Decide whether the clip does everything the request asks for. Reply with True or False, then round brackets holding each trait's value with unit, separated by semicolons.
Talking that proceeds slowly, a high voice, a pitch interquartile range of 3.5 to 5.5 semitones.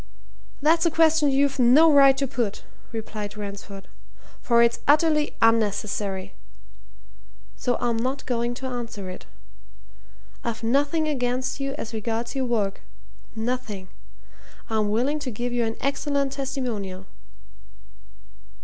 True (120 wpm; 245 Hz; 4.0 semitones)